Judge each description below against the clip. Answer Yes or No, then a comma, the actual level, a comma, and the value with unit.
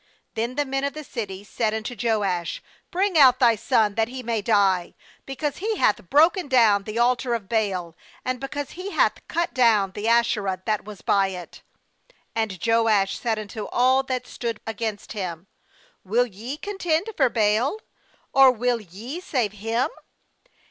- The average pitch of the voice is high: Yes, high, 230 Hz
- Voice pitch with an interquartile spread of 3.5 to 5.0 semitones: Yes, average, 4.1 semitones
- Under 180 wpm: Yes, average, 165 wpm